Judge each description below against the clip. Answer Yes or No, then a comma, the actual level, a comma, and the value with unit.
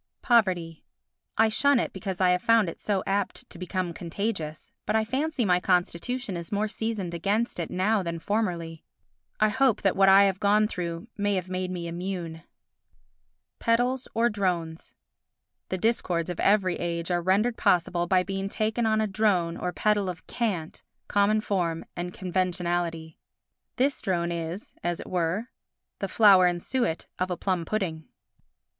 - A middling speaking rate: Yes, average, 165 wpm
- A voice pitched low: No, medium, 185 Hz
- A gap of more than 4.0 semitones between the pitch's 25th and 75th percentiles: No, average, 3.7 semitones